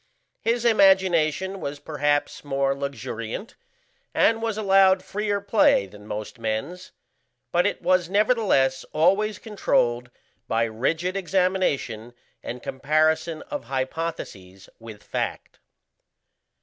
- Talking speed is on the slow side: Yes, slow, 105 wpm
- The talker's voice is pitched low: No, medium, 160 Hz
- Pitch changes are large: Yes, wide, 6.9 semitones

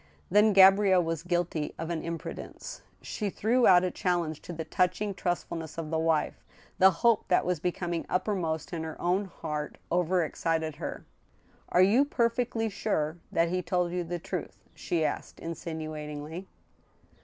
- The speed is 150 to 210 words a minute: Yes, average, 160 wpm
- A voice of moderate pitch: Yes, medium, 175 Hz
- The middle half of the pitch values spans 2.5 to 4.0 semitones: Yes, average, 2.8 semitones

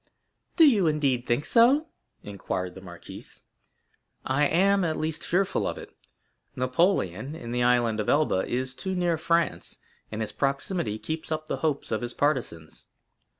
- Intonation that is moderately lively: No, wide, 6.2 semitones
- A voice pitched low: No, medium, 145 Hz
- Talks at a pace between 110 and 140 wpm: No, average, 160 wpm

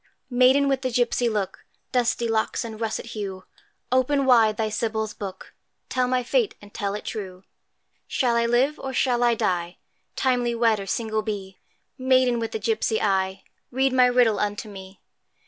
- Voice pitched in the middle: No, high, 230 Hz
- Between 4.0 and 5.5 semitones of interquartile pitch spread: No, average, 3.3 semitones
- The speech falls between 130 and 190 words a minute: Yes, average, 170 wpm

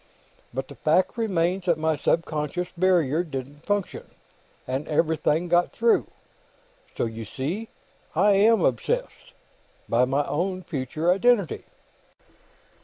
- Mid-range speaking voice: Yes, medium, 165 Hz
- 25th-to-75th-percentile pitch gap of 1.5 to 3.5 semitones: No, average, 4.3 semitones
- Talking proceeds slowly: Yes, slow, 115 wpm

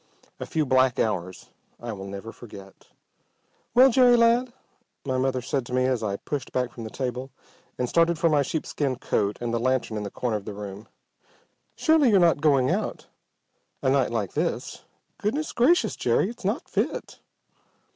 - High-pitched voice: No, low, 130 Hz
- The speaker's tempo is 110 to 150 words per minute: No, average, 175 wpm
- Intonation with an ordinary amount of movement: No, wide, 7.0 semitones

